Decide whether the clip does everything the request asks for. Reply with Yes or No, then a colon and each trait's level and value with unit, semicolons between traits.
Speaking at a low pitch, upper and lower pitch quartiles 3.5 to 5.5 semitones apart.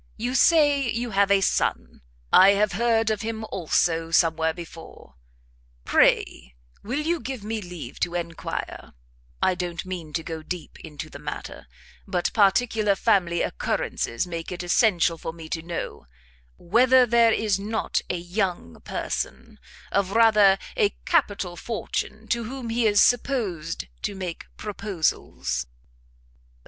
No: high, 195 Hz; average, 4.9 semitones